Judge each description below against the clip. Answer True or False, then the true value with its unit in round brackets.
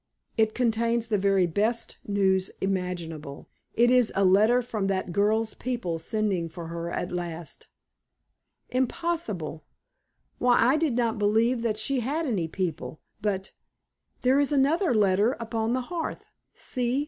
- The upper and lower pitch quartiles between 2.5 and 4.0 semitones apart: False (4.7 semitones)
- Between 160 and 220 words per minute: False (140 wpm)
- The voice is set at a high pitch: True (215 Hz)